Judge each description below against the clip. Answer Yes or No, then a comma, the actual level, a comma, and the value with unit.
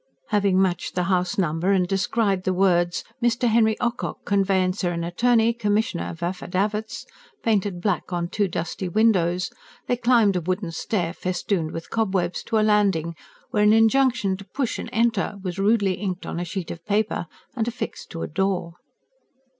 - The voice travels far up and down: No, average, 3.6 semitones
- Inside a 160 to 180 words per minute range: Yes, average, 170 wpm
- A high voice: Yes, high, 195 Hz